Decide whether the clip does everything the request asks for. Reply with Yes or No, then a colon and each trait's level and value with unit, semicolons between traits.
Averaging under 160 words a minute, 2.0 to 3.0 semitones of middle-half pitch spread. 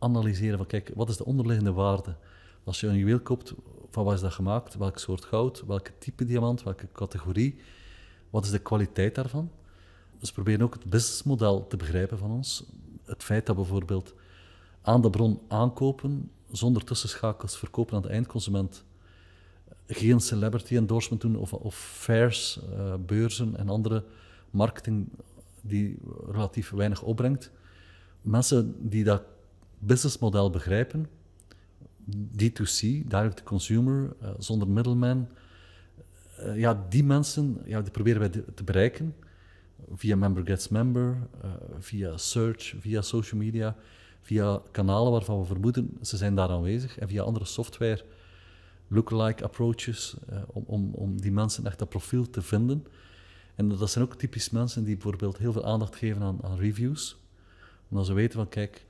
No: average, 150 wpm; average, 3.4 semitones